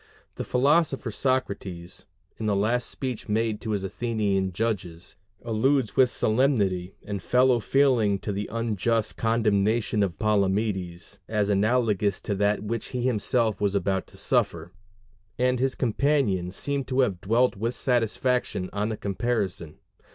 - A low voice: Yes, low, 110 Hz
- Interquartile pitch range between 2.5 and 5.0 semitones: Yes, average, 3.9 semitones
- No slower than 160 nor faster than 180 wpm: No, average, 140 wpm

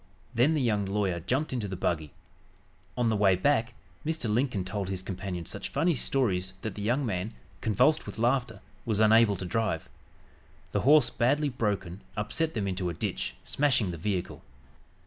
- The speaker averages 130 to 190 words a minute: Yes, average, 170 wpm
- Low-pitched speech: Yes, low, 105 Hz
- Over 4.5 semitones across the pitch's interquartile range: Yes, average, 4.9 semitones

